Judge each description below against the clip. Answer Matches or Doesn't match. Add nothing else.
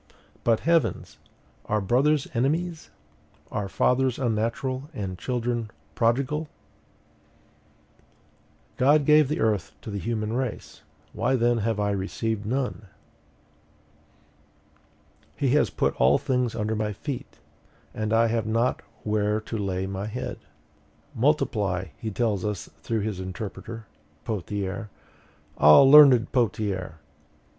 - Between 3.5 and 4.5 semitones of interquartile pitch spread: Matches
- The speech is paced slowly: Matches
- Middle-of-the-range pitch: Doesn't match